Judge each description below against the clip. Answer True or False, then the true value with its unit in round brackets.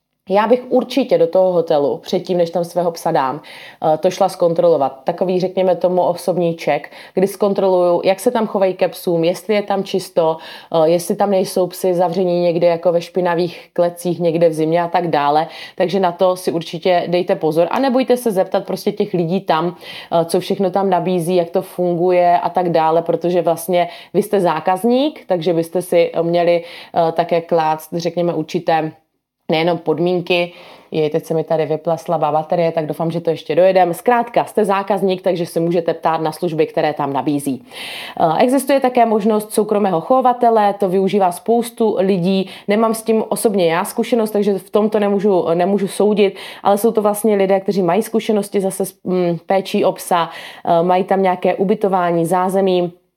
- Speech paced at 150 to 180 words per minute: True (170 wpm)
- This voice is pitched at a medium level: True (180 Hz)